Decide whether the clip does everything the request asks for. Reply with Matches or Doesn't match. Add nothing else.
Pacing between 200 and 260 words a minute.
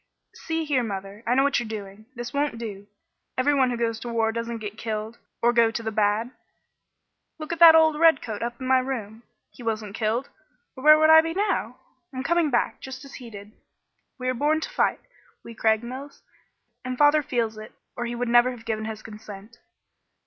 Matches